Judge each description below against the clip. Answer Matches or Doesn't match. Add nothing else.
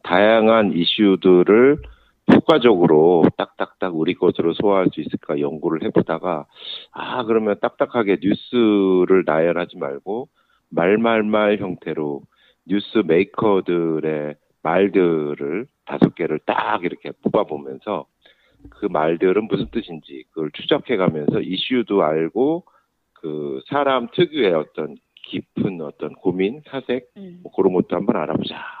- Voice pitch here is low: Matches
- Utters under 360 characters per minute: Matches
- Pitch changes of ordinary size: Doesn't match